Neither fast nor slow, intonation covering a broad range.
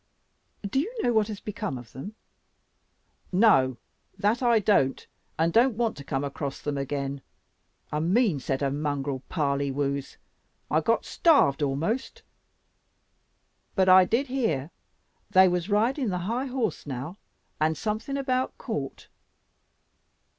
No: slow, 130 wpm; wide, 8.5 semitones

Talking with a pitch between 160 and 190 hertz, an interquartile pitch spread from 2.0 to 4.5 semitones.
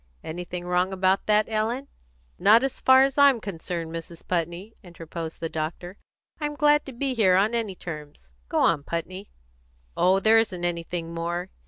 No: medium, 185 Hz; average, 4.9 semitones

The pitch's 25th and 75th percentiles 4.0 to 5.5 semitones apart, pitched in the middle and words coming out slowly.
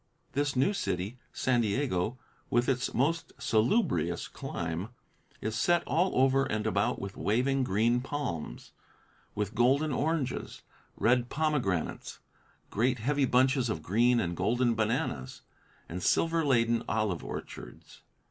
No: average, 4.5 semitones; low, 120 Hz; slow, 125 wpm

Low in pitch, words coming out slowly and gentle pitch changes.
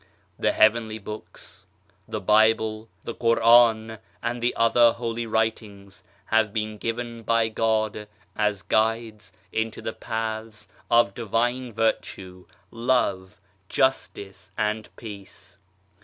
Yes: low, 110 Hz; slow, 110 wpm; narrow, 1.4 semitones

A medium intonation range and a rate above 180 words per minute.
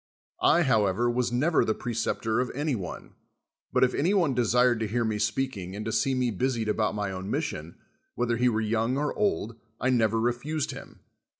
Yes: average, 3.1 semitones; average, 200 wpm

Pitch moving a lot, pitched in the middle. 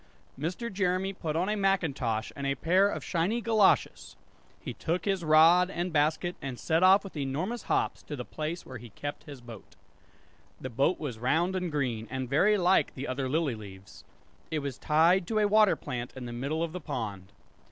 Yes: wide, 5.9 semitones; medium, 155 Hz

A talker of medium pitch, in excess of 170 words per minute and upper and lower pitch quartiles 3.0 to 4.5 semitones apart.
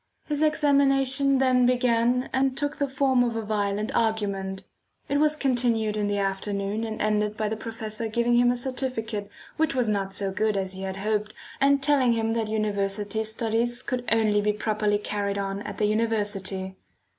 No: high, 220 Hz; average, 180 wpm; average, 3.5 semitones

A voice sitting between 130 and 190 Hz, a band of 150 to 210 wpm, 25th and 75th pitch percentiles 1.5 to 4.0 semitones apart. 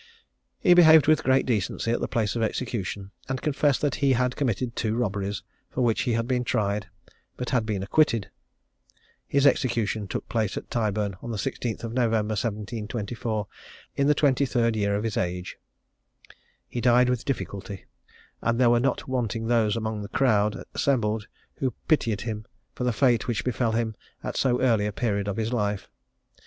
No: low, 115 Hz; average, 180 wpm; average, 3.1 semitones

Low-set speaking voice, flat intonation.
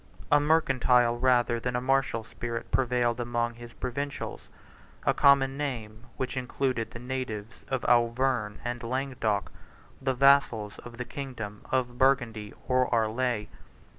Yes: low, 125 Hz; narrow, 2.1 semitones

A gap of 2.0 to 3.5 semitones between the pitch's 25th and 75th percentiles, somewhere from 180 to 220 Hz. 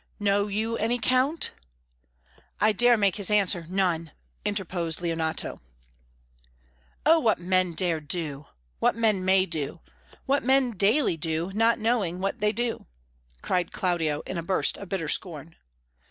No: average, 4.7 semitones; high, 190 Hz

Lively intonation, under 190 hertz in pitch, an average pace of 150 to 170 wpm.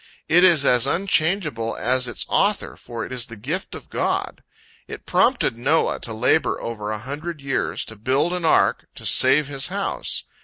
No: wide, 5.8 semitones; low, 135 Hz; average, 180 wpm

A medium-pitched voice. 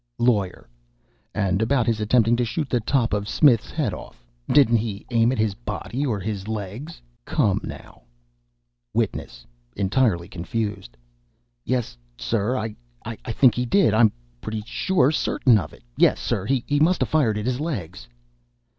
No: low, 110 Hz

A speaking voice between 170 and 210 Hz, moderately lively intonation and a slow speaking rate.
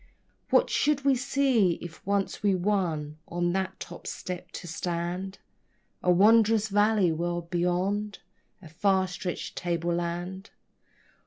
Yes: medium, 185 Hz; average, 3.1 semitones; slow, 120 wpm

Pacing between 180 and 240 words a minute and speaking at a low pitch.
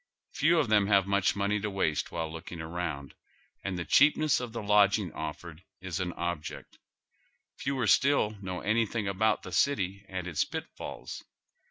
No: average, 160 wpm; low, 100 Hz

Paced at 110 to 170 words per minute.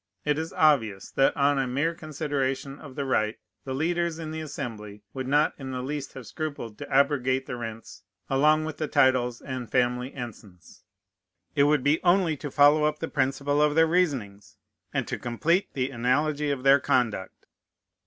No: average, 180 wpm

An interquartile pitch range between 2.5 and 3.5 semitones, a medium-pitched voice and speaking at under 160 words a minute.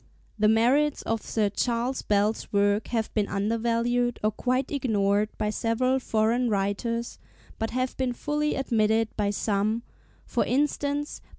No: average, 3.1 semitones; high, 225 Hz; average, 150 wpm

